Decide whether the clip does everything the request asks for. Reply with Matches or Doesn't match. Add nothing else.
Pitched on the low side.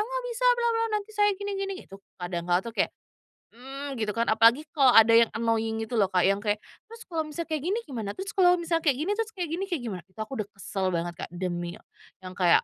Doesn't match